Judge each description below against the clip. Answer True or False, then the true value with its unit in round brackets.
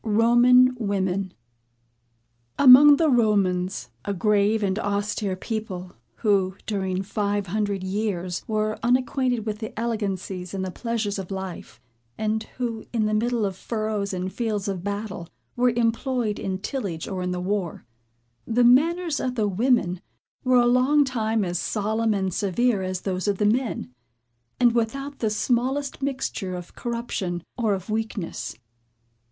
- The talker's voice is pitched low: False (215 Hz)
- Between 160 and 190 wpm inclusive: False (145 wpm)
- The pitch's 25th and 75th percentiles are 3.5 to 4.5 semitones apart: True (3.9 semitones)